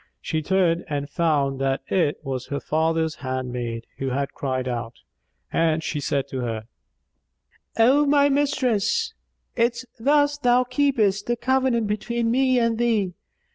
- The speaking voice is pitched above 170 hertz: Yes, high, 190 Hz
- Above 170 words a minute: No, average, 140 wpm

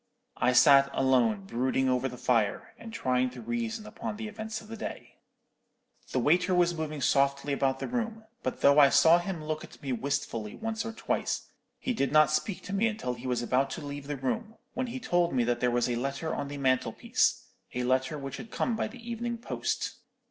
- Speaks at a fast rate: Yes, fast, 215 wpm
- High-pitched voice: No, medium, 145 Hz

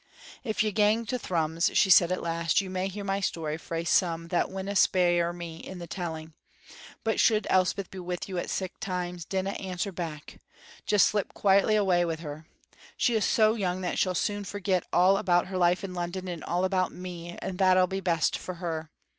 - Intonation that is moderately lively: No, narrow, 2.1 semitones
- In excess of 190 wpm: Yes, average, 200 wpm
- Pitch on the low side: No, medium, 185 Hz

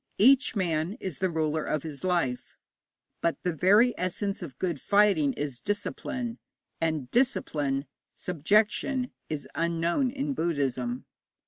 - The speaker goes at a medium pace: No, slow, 125 wpm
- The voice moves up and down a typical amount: No, wide, 5.7 semitones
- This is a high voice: No, medium, 170 Hz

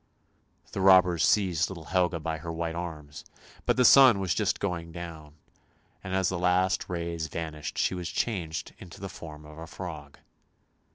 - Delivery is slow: No, average, 170 wpm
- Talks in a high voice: No, very low, 85 Hz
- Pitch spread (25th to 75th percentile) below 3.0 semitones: Yes, narrow, 2.5 semitones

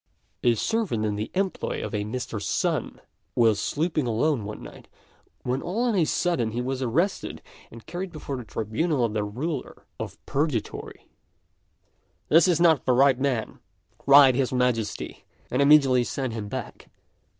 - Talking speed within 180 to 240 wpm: No, average, 160 wpm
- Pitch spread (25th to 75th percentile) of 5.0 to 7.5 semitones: Yes, wide, 5.5 semitones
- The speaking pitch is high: No, low, 130 Hz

